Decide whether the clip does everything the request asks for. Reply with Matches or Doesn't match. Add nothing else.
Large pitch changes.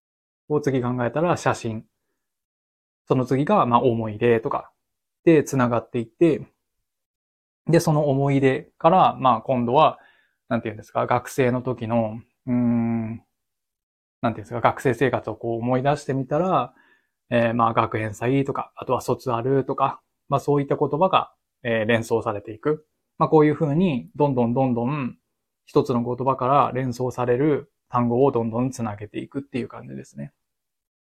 Doesn't match